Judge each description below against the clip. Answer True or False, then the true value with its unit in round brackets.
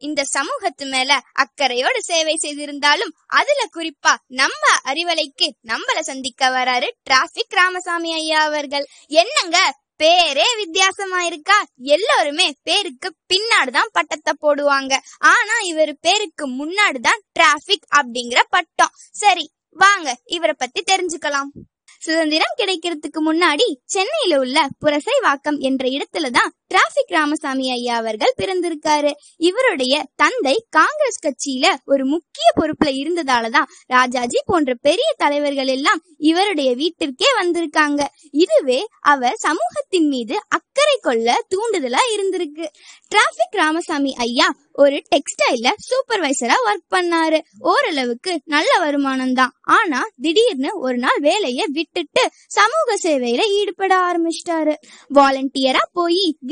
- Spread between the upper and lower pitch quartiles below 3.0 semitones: False (4.3 semitones)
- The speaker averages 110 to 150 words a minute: False (100 wpm)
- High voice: True (315 Hz)